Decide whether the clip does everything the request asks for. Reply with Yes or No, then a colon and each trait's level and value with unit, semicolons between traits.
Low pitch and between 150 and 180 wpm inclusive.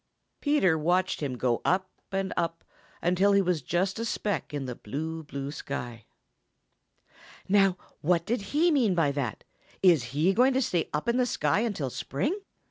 No: medium, 175 Hz; average, 170 wpm